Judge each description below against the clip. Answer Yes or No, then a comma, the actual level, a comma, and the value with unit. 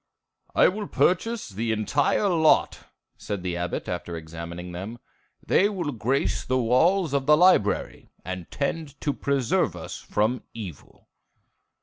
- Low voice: Yes, low, 125 Hz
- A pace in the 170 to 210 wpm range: No, slow, 135 wpm